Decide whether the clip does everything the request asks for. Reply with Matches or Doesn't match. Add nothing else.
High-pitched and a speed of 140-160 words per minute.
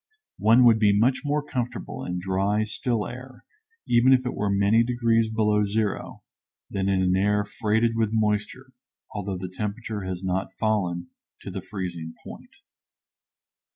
Doesn't match